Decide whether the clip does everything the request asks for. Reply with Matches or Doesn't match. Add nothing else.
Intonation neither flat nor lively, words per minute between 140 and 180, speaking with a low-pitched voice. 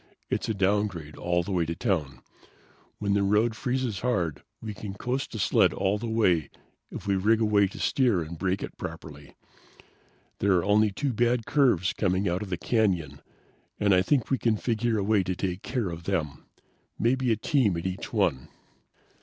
Doesn't match